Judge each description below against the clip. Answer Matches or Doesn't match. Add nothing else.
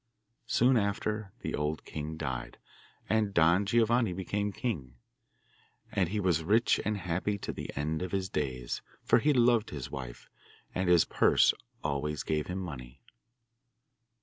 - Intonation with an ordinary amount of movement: Doesn't match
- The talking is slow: Doesn't match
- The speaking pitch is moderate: Doesn't match